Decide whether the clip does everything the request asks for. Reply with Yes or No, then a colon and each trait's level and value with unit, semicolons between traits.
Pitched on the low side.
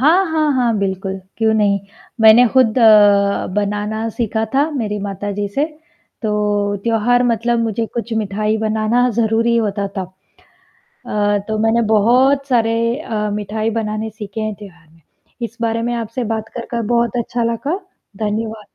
No: high, 220 Hz